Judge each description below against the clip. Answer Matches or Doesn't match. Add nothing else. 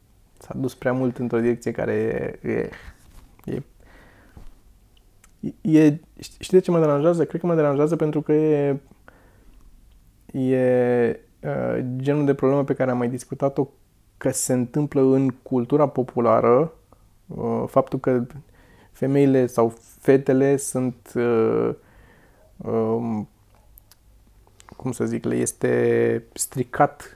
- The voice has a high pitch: Doesn't match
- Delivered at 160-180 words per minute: Doesn't match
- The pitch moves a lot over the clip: Doesn't match